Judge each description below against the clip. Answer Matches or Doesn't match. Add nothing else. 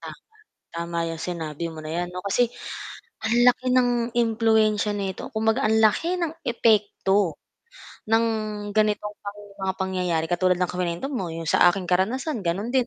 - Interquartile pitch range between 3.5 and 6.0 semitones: Matches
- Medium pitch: Doesn't match